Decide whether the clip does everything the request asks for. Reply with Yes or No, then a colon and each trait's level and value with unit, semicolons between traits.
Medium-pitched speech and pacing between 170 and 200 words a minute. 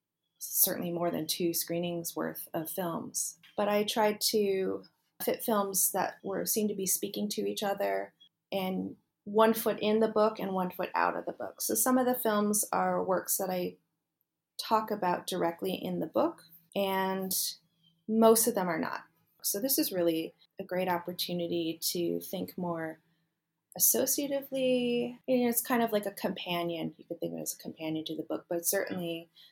Yes: medium, 180 Hz; average, 180 wpm